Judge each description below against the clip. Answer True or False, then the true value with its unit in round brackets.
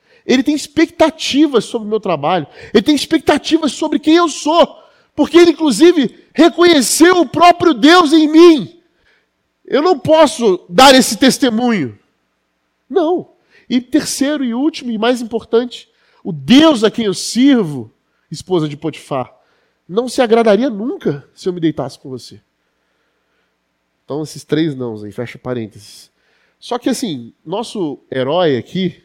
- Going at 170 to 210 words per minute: False (145 wpm)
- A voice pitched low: False (245 Hz)